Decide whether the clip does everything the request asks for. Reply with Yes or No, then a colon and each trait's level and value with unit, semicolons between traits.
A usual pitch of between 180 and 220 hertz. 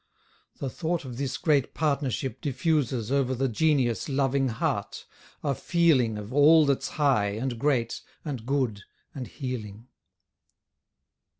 No: low, 135 Hz